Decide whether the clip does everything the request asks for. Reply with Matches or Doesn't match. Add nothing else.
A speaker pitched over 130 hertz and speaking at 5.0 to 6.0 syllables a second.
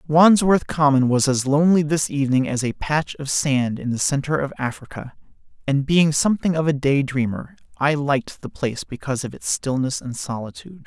Matches